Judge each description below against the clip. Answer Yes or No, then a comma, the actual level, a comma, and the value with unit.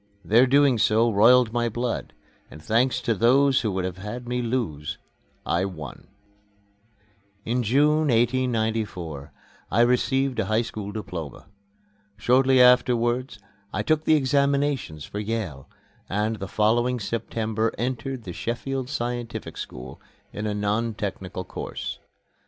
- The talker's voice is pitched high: No, low, 115 Hz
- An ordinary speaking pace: No, slow, 130 wpm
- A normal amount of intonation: Yes, average, 3.5 semitones